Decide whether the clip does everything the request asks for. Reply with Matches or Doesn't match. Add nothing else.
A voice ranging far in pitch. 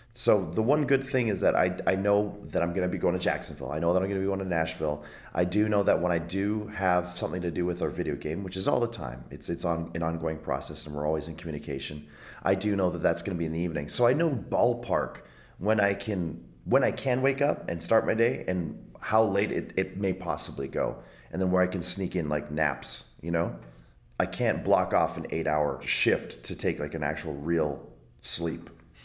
Doesn't match